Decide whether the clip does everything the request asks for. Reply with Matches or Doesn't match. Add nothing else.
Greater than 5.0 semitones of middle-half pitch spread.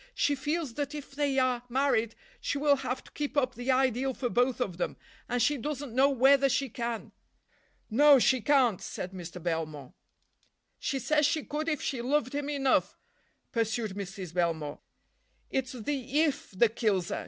Doesn't match